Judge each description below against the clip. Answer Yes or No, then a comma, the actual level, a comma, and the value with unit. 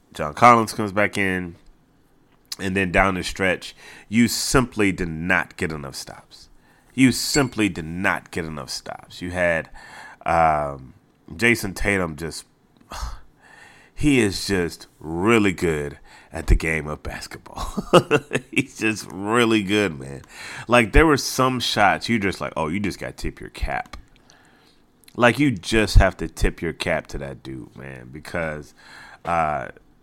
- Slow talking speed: No, average, 150 wpm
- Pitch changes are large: Yes, wide, 5.9 semitones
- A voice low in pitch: Yes, very low, 95 Hz